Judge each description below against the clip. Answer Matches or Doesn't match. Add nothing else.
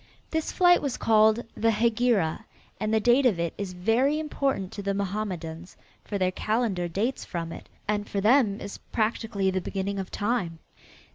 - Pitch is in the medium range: Doesn't match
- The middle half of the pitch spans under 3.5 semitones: Doesn't match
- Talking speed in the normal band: Matches